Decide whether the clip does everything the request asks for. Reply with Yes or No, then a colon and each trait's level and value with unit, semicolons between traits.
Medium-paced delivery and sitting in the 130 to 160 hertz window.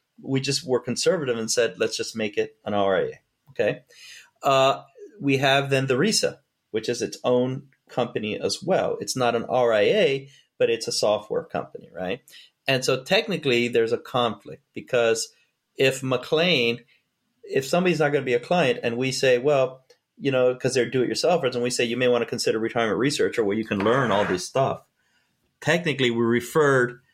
Yes: average, 190 wpm; low, 135 Hz